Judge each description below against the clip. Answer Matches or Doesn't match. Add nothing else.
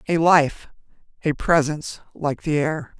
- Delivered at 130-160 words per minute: Matches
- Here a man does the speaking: Doesn't match